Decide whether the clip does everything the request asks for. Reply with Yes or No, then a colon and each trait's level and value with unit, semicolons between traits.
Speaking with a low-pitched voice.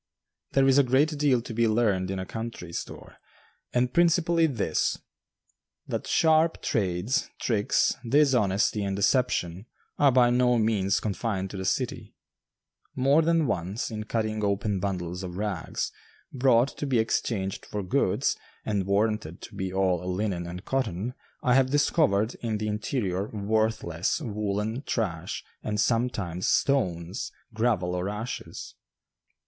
Yes: low, 110 Hz